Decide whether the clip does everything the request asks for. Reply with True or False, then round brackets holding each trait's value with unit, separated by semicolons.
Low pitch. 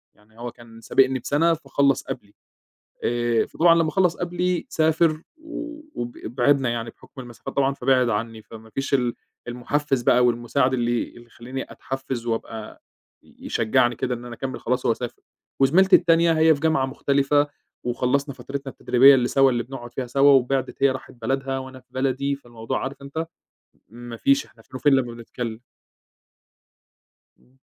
True (130 Hz)